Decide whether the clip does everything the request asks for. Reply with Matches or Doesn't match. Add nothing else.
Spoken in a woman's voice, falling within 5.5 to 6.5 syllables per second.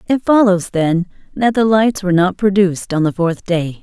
Doesn't match